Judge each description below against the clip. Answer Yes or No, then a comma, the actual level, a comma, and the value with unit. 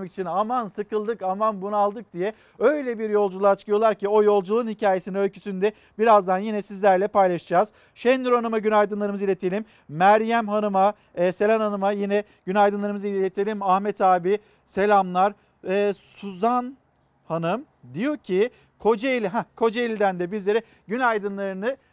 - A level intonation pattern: Yes, narrow, 1.9 semitones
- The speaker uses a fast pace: No, average, 125 wpm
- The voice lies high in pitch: Yes, high, 205 Hz